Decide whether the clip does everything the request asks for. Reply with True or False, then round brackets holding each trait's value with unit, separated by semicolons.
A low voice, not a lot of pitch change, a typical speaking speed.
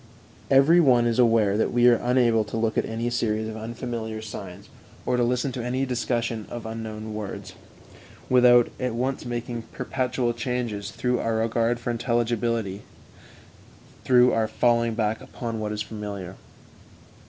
True (115 Hz; 1.9 semitones; 155 wpm)